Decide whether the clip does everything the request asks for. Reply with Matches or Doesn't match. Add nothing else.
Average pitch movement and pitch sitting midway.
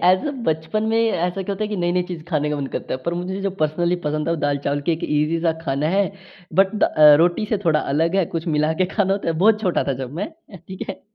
Matches